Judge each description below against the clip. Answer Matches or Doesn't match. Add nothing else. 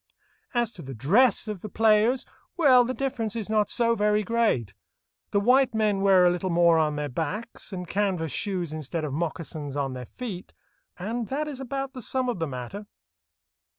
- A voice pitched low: Doesn't match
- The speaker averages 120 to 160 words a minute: Doesn't match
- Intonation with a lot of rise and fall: Matches